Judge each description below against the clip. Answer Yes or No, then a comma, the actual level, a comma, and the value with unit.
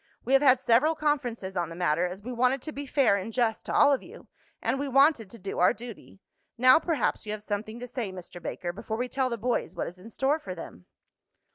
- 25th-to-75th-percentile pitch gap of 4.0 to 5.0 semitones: No, wide, 5.5 semitones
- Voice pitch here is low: No, high, 235 Hz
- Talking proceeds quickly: Yes, fast, 245 wpm